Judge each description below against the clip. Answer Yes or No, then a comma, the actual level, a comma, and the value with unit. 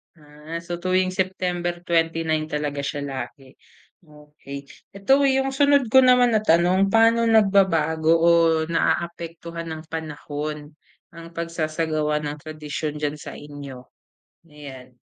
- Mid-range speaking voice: Yes, medium, 165 Hz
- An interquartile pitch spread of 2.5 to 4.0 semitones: Yes, average, 3.7 semitones